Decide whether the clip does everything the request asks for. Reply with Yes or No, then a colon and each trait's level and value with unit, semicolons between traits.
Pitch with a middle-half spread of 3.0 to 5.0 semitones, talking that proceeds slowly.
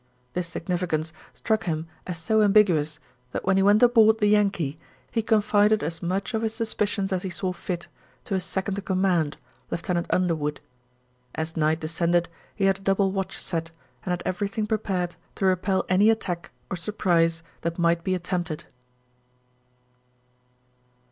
No: average, 3.3 semitones; average, 155 wpm